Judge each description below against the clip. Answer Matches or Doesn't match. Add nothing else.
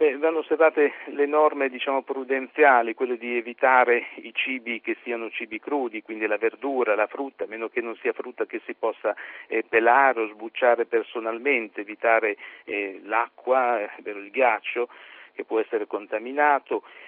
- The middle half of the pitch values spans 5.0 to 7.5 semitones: Matches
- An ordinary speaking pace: Matches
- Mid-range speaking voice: Doesn't match